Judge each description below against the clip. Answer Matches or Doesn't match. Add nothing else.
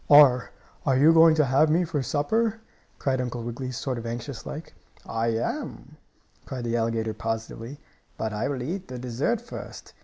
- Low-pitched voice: Matches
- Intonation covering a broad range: Doesn't match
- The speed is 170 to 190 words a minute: Matches